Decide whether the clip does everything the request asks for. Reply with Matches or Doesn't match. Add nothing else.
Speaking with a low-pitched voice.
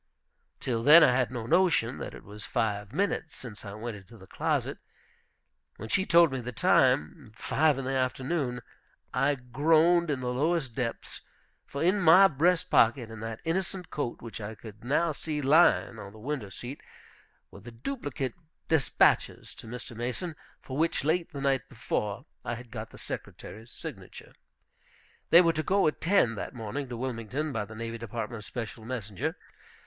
Matches